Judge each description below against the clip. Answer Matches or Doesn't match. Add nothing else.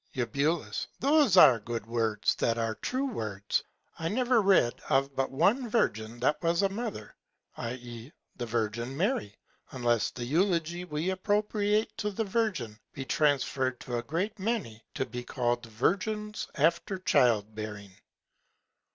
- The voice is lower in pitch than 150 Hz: Matches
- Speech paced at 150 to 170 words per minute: Doesn't match